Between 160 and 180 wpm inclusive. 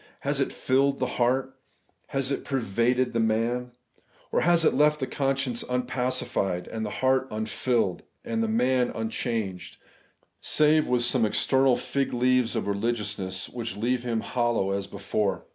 No: average, 145 wpm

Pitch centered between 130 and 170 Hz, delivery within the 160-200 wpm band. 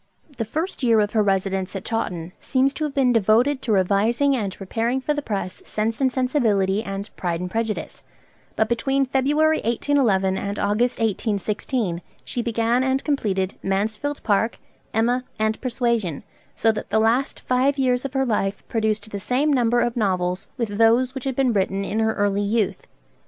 No: high, 225 Hz; average, 175 wpm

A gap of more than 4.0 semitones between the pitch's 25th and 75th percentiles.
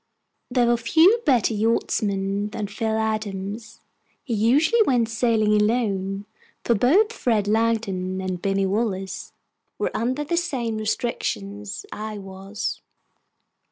No: average, 3.2 semitones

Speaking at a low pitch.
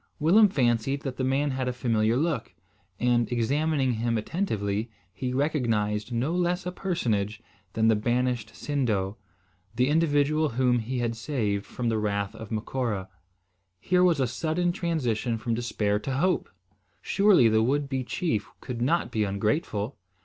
Yes: low, 125 Hz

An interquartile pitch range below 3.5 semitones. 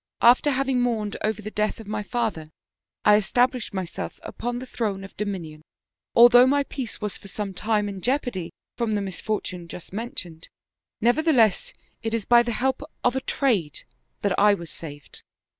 No: average, 3.9 semitones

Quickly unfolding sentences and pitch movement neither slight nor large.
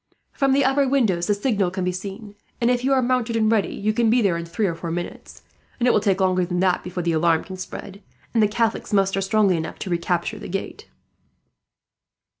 Yes: fast, 225 wpm; average, 4.1 semitones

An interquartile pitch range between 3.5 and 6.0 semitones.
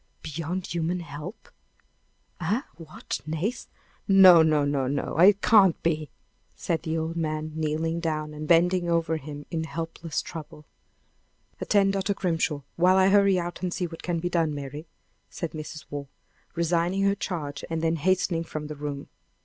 No: narrow, 2.6 semitones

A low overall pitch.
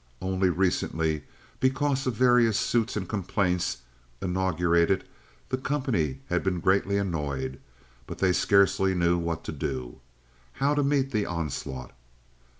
Yes: very low, 95 Hz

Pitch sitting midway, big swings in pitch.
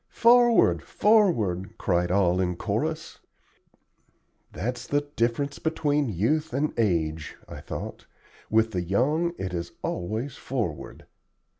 No: low, 115 Hz; wide, 8.7 semitones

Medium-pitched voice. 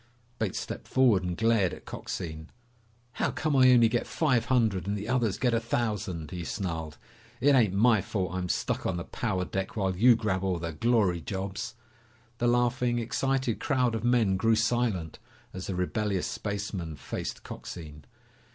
No: low, 105 Hz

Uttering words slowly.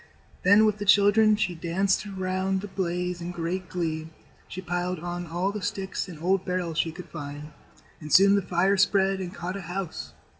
No: average, 190 wpm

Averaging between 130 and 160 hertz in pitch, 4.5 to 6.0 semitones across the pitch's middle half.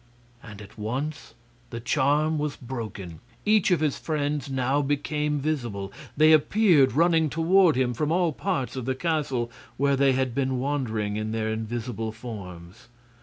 Yes: low, 135 Hz; average, 5.0 semitones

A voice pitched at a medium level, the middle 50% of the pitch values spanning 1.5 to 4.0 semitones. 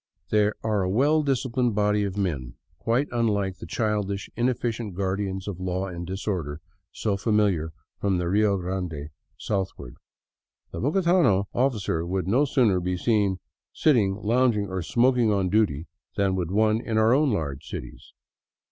No: low, 100 Hz; average, 3.6 semitones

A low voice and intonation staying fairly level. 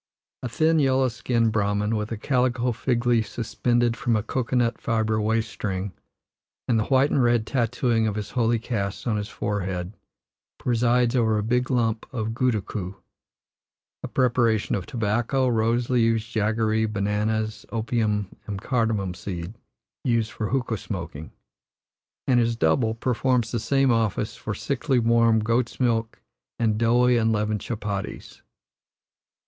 Yes: low, 115 Hz; narrow, 2.2 semitones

